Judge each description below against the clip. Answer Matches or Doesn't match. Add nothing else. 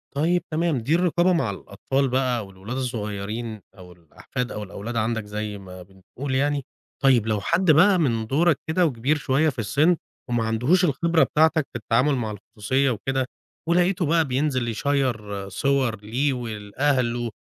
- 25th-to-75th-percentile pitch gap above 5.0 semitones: Matches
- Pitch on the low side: Matches